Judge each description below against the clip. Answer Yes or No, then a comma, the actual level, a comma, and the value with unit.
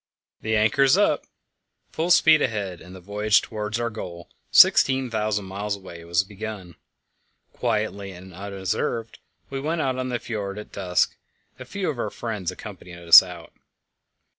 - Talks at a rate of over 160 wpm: No, average, 150 wpm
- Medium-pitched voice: No, low, 105 Hz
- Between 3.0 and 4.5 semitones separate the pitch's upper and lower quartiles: Yes, average, 3.9 semitones